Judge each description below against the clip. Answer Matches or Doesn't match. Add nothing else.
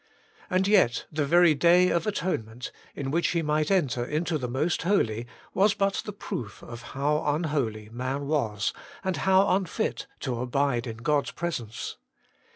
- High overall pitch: Doesn't match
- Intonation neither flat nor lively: Doesn't match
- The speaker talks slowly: Doesn't match